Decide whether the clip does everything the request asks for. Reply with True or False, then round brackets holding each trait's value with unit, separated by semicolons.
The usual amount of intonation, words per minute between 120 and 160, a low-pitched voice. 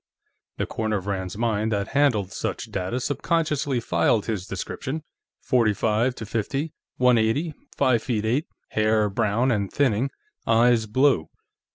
True (3.8 semitones; 145 wpm; 115 Hz)